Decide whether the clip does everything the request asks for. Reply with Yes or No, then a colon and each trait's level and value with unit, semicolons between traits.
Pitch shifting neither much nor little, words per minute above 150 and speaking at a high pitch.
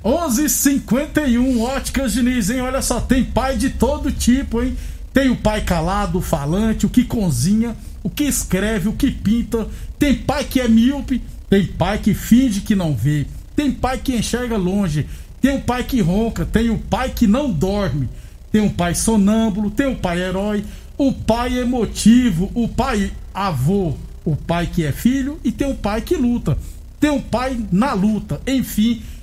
Yes: average, 4.5 semitones; average, 180 wpm; high, 225 Hz